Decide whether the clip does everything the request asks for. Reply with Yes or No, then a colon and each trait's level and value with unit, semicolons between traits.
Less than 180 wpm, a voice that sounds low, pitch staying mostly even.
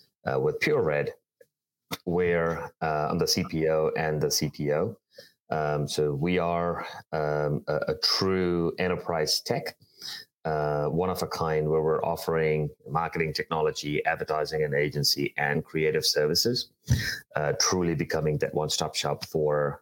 Yes: slow, 135 wpm; very low, 80 Hz; narrow, 2.3 semitones